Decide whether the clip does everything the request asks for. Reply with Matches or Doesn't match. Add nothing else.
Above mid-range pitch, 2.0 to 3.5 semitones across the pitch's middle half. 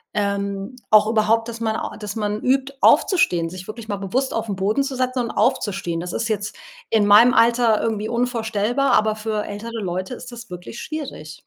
Matches